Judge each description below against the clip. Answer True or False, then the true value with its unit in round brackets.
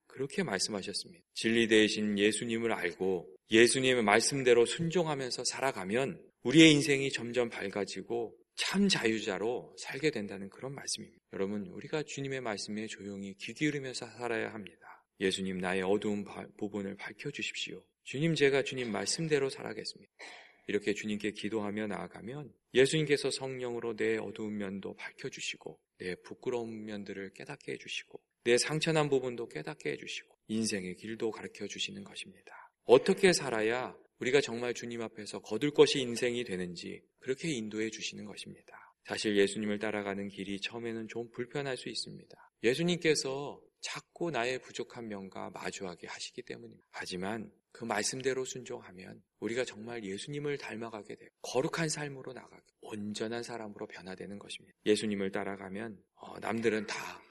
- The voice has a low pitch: True (115 Hz)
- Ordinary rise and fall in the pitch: True (4.2 semitones)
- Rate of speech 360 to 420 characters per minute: True (375 characters per minute)